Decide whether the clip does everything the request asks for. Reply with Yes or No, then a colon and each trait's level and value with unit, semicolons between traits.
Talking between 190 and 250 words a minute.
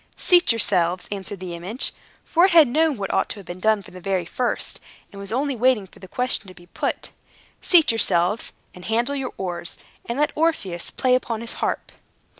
Yes: fast, 205 wpm